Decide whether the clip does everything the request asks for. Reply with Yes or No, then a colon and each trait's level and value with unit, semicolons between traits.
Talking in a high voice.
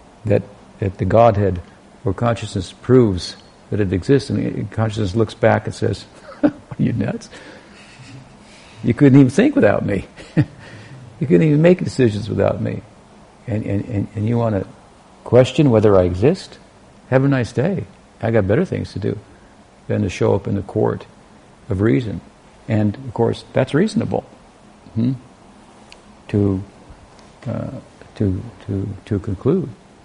No: low, 110 Hz